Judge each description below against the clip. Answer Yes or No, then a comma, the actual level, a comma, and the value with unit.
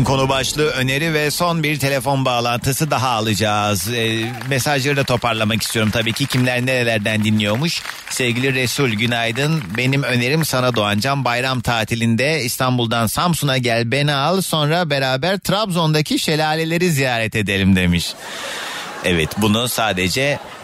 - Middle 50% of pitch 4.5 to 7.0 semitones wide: No, average, 4.1 semitones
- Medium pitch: No, low, 130 Hz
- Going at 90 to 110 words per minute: No, average, 130 wpm